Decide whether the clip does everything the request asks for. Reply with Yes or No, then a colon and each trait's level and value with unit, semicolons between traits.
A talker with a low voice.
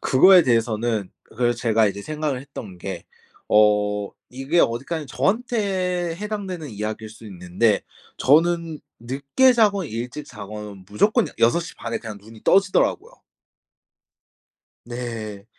Yes: low, 125 Hz